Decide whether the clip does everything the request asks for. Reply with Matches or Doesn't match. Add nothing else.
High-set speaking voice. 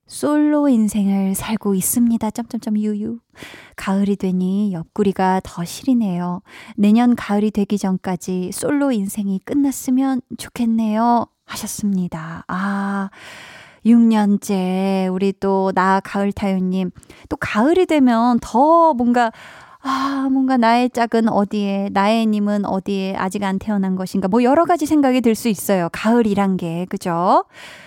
Matches